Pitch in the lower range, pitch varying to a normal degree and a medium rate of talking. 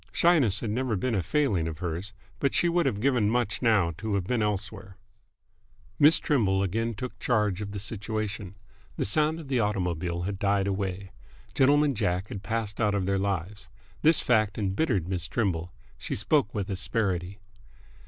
Yes: low, 105 Hz; average, 3.7 semitones; average, 175 wpm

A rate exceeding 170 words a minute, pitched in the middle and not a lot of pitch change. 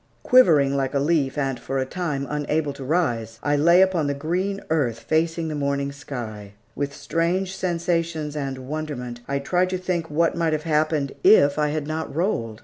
No: average, 185 wpm; medium, 150 Hz; average, 3.2 semitones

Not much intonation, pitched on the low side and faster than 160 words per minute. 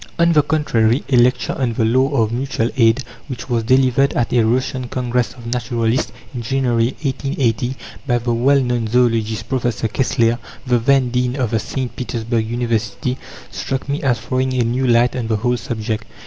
Yes: narrow, 2.1 semitones; low, 120 Hz; average, 180 wpm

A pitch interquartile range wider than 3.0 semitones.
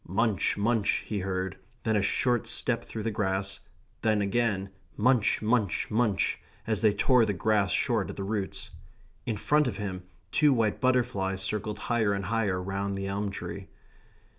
No: narrow, 2.6 semitones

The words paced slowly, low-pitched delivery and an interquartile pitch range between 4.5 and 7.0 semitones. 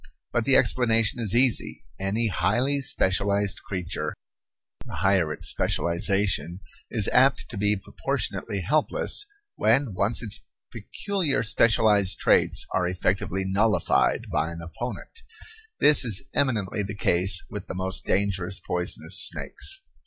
No: slow, 125 wpm; low, 100 Hz; average, 4.0 semitones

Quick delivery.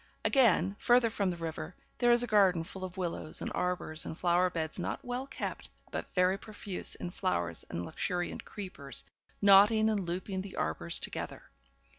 No: average, 170 wpm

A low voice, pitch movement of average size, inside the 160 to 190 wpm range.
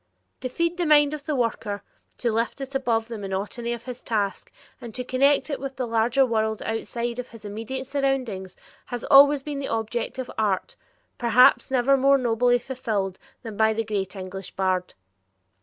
No: high, 240 Hz; average, 3.5 semitones; average, 180 wpm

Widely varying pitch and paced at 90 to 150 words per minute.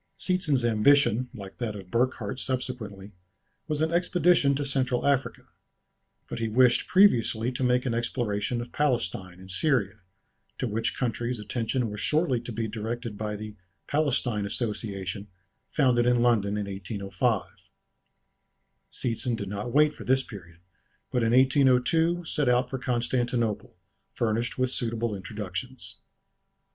No: average, 3.6 semitones; slow, 135 wpm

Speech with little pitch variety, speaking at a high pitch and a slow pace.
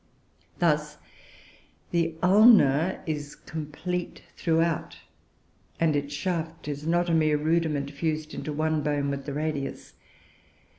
No: narrow, 2.2 semitones; medium, 155 Hz; slow, 115 wpm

